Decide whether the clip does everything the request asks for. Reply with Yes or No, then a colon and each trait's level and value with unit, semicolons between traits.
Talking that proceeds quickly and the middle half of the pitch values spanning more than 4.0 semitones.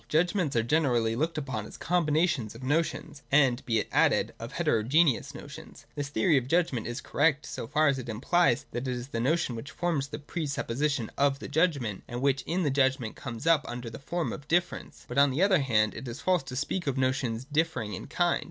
Yes: fast, 215 wpm; average, 4.7 semitones